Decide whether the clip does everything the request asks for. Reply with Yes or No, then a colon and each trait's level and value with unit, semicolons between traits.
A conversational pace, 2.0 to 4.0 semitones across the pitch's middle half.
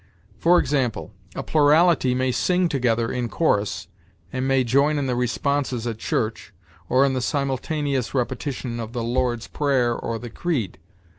Yes: average, 155 wpm; average, 3.1 semitones